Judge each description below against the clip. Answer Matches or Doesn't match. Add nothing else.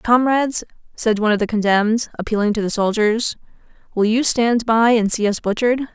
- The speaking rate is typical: Matches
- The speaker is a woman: Matches